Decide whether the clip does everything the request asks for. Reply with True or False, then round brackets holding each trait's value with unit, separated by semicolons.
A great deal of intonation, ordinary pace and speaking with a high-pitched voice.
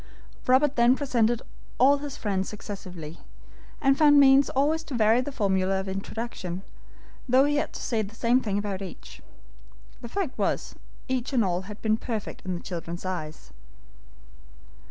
True (5.8 semitones; 160 wpm; 225 Hz)